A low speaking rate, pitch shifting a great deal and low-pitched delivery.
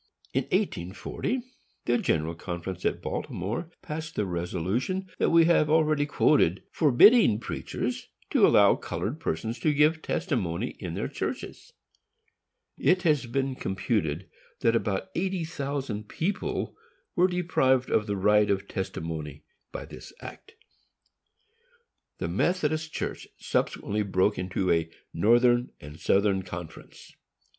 Yes: slow, 125 wpm; wide, 8.8 semitones; low, 115 Hz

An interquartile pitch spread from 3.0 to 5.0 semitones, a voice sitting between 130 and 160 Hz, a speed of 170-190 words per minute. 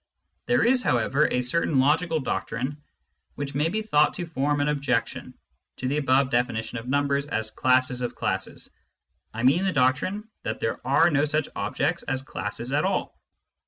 Yes: average, 3.3 semitones; medium, 140 Hz; average, 175 wpm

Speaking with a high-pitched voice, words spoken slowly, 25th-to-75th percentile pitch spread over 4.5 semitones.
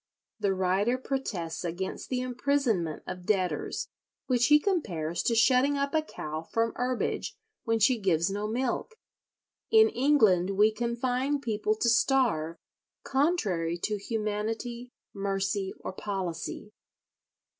Yes: high, 220 Hz; slow, 125 wpm; average, 5.1 semitones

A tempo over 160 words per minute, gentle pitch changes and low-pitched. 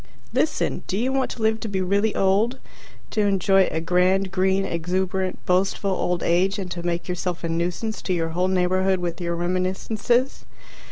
No: average, 175 wpm; narrow, 1.8 semitones; medium, 185 Hz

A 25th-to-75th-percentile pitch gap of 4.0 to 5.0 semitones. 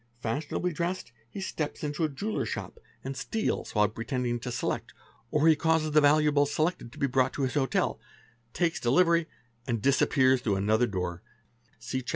Yes: average, 4.7 semitones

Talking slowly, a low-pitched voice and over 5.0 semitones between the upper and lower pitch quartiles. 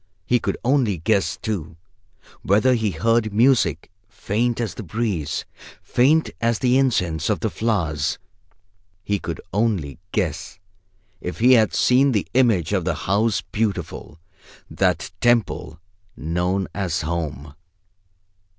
Yes: slow, 125 wpm; low, 105 Hz; wide, 5.6 semitones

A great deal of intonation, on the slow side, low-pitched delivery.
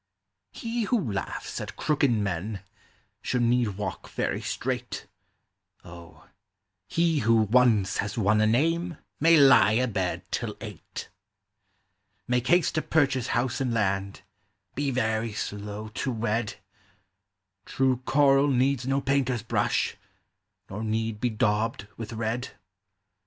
No: average, 4.0 semitones; slow, 125 wpm; low, 120 Hz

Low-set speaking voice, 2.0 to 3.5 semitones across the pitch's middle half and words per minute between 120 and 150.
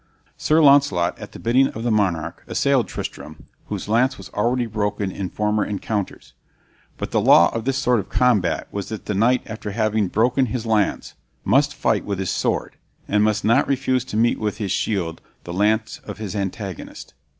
No: low, 110 Hz; average, 3.2 semitones; average, 185 wpm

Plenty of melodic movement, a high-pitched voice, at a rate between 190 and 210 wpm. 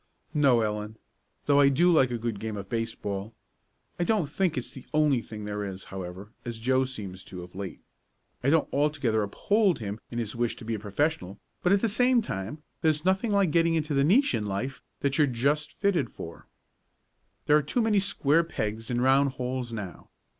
No: wide, 6.5 semitones; low, 130 Hz; average, 200 wpm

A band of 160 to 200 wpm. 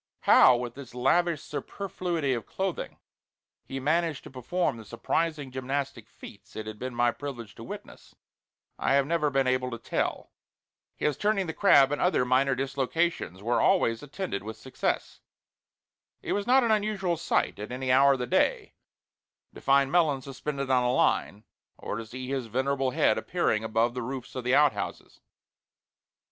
Yes: average, 170 wpm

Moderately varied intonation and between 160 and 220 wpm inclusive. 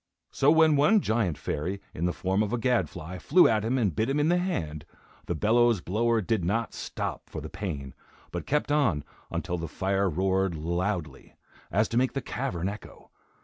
No: wide, 5.8 semitones; average, 190 wpm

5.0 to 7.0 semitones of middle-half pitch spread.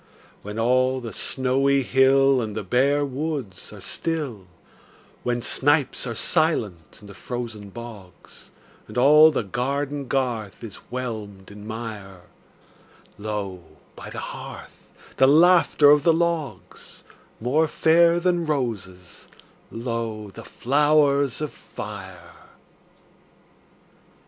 Yes: average, 5.3 semitones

